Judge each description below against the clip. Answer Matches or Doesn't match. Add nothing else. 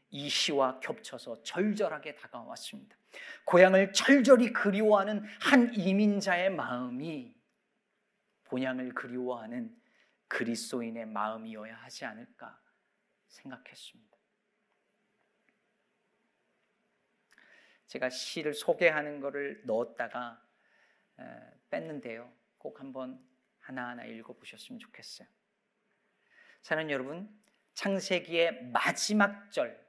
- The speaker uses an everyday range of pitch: Doesn't match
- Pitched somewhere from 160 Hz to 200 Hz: Matches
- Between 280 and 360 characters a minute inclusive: Doesn't match